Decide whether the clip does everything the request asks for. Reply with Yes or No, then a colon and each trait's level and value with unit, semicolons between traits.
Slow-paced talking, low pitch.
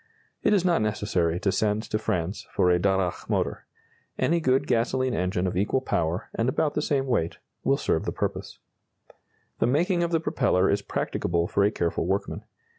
No: average, 185 wpm; low, 105 Hz